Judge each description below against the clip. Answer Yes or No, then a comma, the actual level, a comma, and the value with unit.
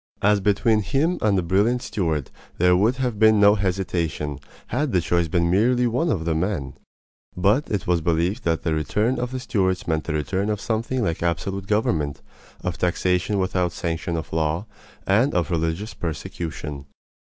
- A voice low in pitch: Yes, very low, 95 Hz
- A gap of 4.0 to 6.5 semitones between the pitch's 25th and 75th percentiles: Yes, average, 4.6 semitones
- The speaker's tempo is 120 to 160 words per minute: No, average, 170 wpm